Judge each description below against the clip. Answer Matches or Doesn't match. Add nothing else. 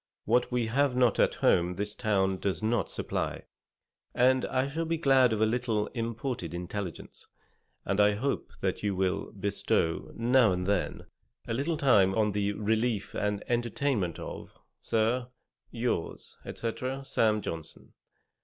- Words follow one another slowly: Doesn't match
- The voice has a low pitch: Matches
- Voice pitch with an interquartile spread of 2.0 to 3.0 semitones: Doesn't match